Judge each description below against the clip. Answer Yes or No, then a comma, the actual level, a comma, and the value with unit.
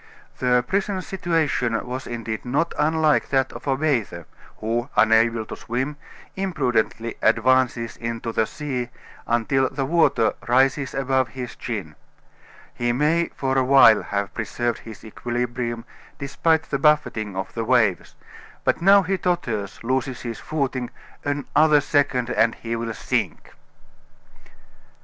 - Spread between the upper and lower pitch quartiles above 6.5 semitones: No, average, 3.8 semitones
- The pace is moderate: No, slow, 130 wpm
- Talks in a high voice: No, low, 125 Hz